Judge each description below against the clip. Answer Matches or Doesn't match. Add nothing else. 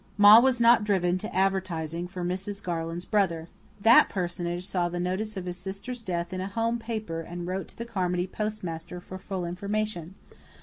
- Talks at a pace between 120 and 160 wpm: Doesn't match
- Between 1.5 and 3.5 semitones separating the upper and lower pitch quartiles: Matches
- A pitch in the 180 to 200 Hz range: Matches